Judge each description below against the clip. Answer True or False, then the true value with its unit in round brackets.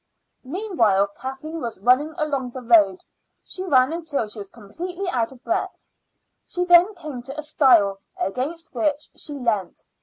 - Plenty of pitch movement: True (6.1 semitones)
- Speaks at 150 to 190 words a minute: True (155 wpm)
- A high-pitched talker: True (270 Hz)